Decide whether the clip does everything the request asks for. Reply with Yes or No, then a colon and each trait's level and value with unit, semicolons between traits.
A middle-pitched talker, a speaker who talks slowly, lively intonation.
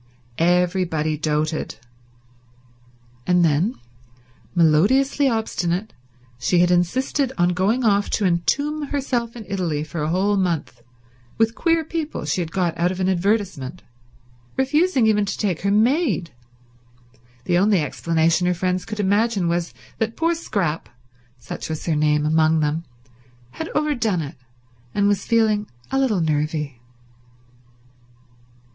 Yes: medium, 180 Hz; slow, 125 wpm; wide, 5.8 semitones